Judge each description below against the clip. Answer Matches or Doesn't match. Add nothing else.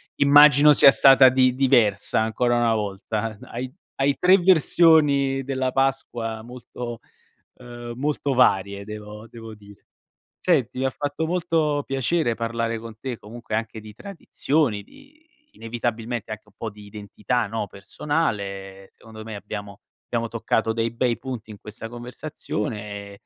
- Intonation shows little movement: Doesn't match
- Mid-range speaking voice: Doesn't match